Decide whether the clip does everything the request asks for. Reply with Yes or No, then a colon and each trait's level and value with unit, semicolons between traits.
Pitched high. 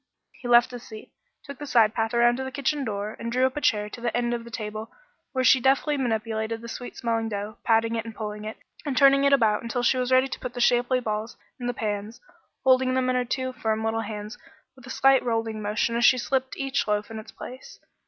Yes: high, 235 Hz